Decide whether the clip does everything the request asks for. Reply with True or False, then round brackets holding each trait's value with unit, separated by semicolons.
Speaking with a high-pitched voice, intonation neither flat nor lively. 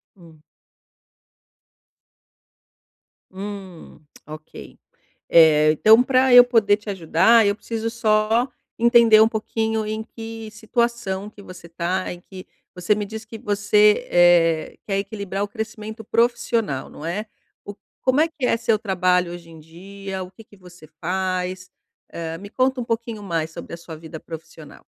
True (205 Hz; 4.1 semitones)